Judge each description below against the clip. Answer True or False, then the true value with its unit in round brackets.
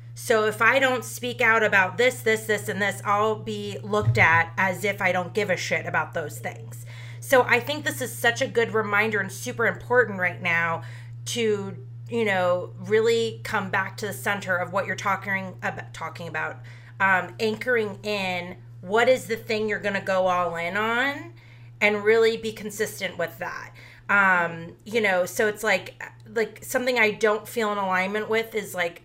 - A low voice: False (195 Hz)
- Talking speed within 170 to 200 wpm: True (190 wpm)